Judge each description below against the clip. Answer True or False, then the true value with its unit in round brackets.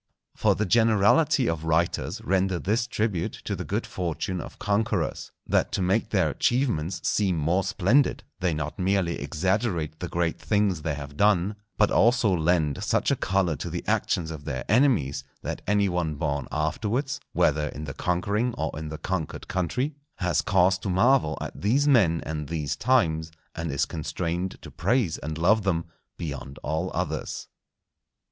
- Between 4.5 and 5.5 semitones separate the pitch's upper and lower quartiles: True (4.8 semitones)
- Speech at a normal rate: True (165 wpm)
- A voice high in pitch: False (90 Hz)